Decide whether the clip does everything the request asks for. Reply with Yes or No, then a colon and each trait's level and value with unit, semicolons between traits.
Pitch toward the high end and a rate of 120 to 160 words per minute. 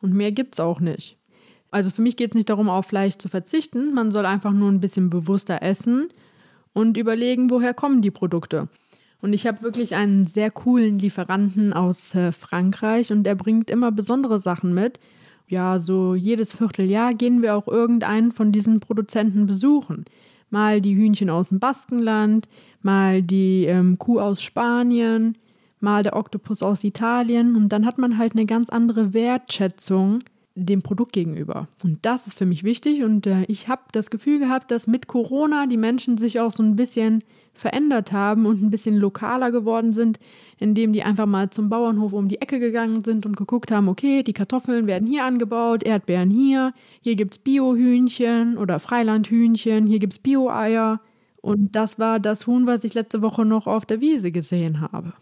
No: high, 220 Hz; average, 180 wpm